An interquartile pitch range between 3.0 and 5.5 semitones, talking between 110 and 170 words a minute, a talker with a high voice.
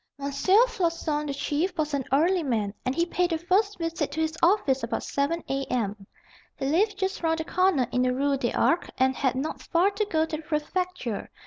No: average, 4.8 semitones; fast, 205 wpm; very high, 315 Hz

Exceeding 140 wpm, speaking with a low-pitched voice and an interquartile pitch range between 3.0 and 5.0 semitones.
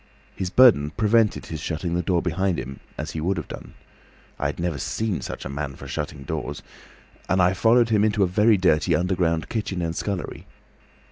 Yes: average, 180 wpm; very low, 90 Hz; average, 4.4 semitones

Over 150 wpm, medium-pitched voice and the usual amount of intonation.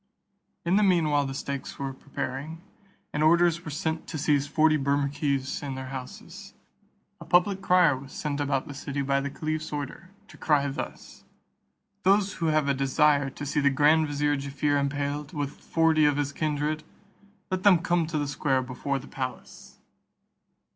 No: average, 175 wpm; medium, 145 Hz; narrow, 2.2 semitones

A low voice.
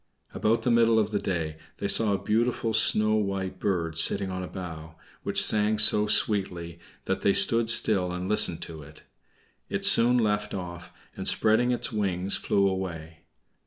Yes: low, 100 Hz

